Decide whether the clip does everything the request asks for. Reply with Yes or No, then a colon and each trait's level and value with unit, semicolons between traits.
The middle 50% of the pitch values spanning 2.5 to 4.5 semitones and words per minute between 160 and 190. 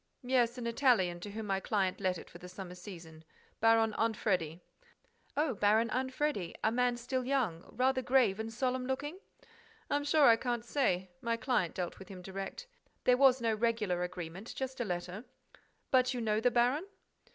No: average, 5.2 semitones; average, 175 wpm